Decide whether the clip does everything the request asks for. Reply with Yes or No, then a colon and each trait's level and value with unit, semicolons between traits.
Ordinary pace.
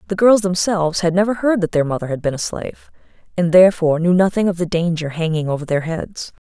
No: fast, 225 wpm